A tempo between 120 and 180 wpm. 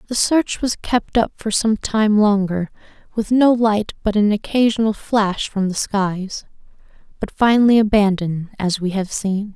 Yes: average, 165 wpm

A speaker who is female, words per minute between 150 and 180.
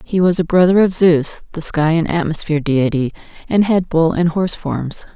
No: female; average, 200 wpm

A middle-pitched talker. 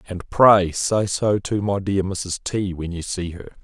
No: very low, 95 Hz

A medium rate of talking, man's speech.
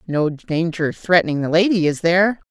No: average, 165 wpm; female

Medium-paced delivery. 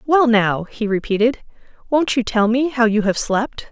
Yes: average, 195 wpm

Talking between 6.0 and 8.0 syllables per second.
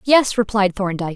No: 5.7 syllables/s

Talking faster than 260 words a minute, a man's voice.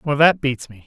Yes: fast, 280 wpm; male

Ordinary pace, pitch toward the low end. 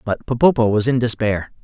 Yes: average, 185 wpm; low, 115 Hz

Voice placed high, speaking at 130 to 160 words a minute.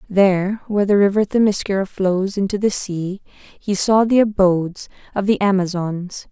Yes: high, 195 Hz; average, 150 wpm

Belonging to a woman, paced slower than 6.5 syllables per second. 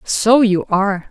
Yes: female; 4.1 syllables/s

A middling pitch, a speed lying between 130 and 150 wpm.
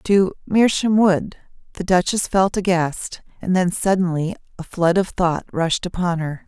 Yes: medium, 180 Hz; average, 140 wpm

